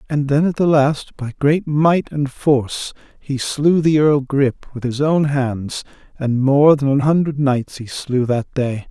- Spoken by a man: Yes, male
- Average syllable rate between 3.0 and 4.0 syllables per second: Yes, 3.9 syllables/s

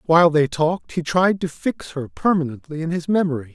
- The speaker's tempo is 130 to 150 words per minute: No, fast, 205 wpm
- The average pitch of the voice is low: No, medium, 160 Hz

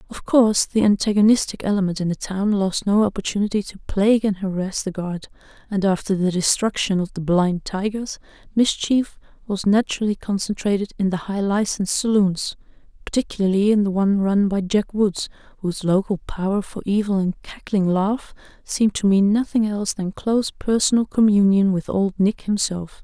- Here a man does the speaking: No, female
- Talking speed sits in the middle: Yes, average, 160 wpm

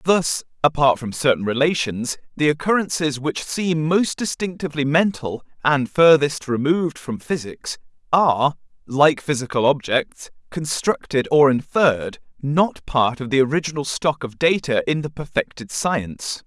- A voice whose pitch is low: No, medium, 145 Hz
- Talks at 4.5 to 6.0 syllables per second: No, 4.2 syllables/s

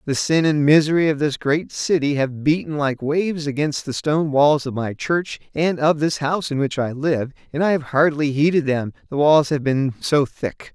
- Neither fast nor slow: No, fast, 220 wpm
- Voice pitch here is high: No, medium, 145 Hz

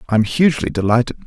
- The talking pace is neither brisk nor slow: Yes, average, 190 wpm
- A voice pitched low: Yes, low, 120 Hz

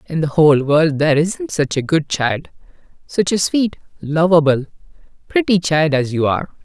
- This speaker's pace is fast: No, average, 170 wpm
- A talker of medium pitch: Yes, medium, 160 Hz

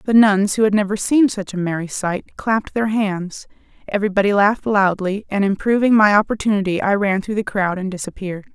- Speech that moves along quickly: No, average, 190 wpm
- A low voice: No, high, 200 Hz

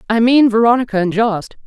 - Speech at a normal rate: Yes, average, 180 wpm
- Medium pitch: No, high, 225 Hz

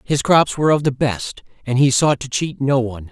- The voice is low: Yes, low, 130 Hz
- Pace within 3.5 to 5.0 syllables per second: No, 5.3 syllables/s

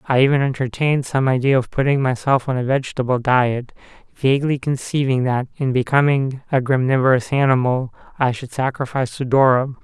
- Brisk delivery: No, average, 150 wpm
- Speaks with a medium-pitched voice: No, low, 130 Hz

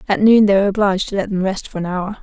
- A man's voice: No, female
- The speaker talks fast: Yes, fast, 325 wpm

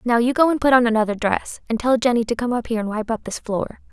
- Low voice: No, high, 235 Hz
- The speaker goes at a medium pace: No, fast, 305 wpm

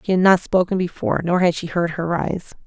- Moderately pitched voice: Yes, medium, 175 Hz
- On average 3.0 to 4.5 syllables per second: No, 5.9 syllables/s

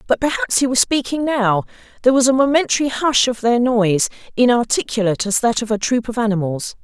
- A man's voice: No, female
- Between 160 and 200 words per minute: Yes, average, 195 wpm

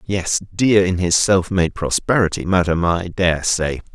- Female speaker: No, male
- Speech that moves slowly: No, average, 165 wpm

